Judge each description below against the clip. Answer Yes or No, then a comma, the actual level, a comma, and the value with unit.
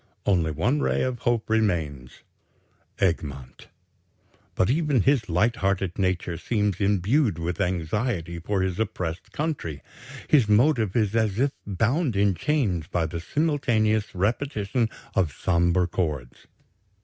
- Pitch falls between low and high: No, low, 100 Hz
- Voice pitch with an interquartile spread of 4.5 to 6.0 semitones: Yes, wide, 5.5 semitones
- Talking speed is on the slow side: Yes, slow, 125 wpm